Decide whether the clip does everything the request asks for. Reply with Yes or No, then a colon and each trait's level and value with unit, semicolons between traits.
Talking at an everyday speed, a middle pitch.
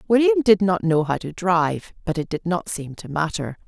No: fast, 230 wpm; medium, 180 Hz